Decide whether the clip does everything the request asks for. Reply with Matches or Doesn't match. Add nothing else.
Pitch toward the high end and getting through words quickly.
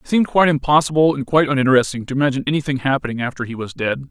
Doesn't match